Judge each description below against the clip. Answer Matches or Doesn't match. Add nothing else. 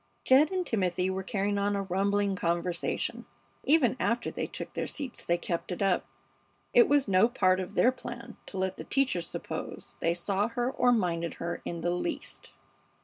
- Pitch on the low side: Doesn't match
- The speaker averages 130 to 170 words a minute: Doesn't match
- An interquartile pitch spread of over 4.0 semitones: Matches